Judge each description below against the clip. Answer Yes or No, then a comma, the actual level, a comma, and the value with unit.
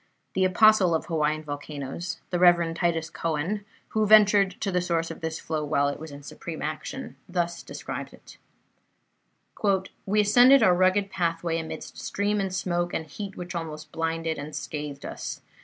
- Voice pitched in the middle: Yes, medium, 170 Hz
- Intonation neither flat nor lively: Yes, average, 3.2 semitones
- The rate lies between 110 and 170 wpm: Yes, average, 165 wpm